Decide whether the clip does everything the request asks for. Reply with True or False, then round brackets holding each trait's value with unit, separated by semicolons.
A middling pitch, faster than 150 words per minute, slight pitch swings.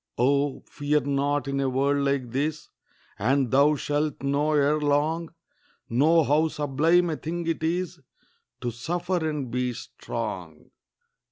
False (145 Hz; 140 wpm; 2.3 semitones)